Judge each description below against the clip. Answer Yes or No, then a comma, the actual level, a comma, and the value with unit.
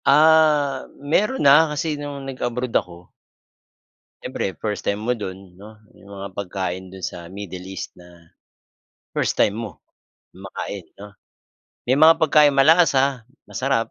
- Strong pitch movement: Yes, wide, 7.0 semitones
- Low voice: Yes, low, 115 Hz